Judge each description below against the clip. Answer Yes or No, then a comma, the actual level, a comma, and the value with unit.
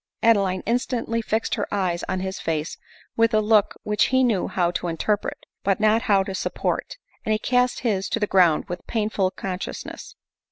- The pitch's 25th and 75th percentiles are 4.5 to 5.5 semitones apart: No, average, 3.3 semitones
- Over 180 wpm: Yes, average, 200 wpm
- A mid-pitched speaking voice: No, high, 205 Hz